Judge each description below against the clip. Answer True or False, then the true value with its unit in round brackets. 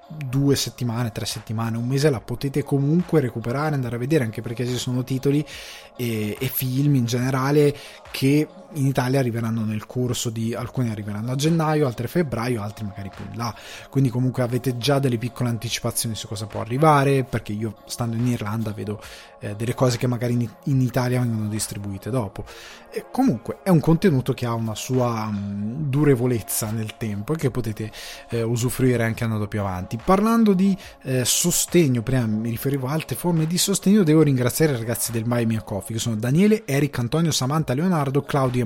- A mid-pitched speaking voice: False (125 Hz)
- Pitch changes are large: False (3.6 semitones)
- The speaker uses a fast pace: True (185 wpm)